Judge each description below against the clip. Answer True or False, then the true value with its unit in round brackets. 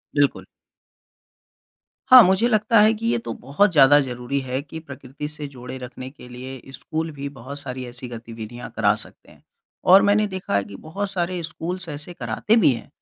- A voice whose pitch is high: False (145 Hz)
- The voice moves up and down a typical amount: False (6.5 semitones)